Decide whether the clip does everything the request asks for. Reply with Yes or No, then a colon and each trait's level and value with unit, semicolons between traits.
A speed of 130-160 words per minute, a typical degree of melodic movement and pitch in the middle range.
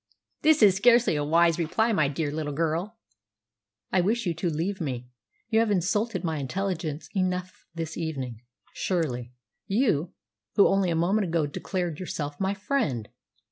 Yes: average, 155 wpm; average, 4.5 semitones; medium, 170 Hz